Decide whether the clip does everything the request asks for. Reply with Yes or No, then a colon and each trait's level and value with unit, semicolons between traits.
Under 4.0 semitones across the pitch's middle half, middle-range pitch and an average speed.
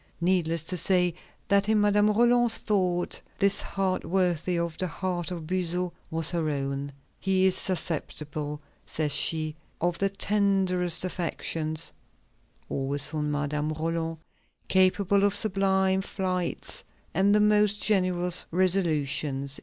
No: average, 3.6 semitones; medium, 180 Hz; slow, 125 wpm